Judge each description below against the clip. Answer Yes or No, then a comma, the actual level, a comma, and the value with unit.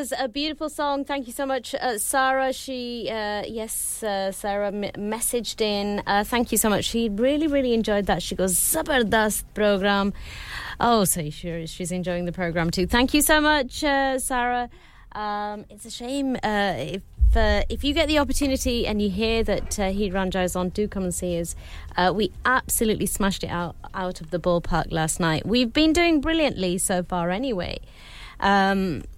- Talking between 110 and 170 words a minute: No, average, 185 wpm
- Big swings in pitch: Yes, wide, 5.7 semitones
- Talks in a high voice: Yes, high, 210 Hz